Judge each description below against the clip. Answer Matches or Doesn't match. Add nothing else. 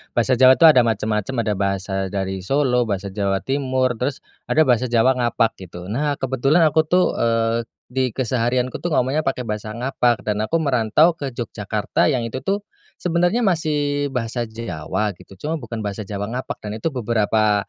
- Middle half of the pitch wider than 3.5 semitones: Matches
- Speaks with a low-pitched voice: Matches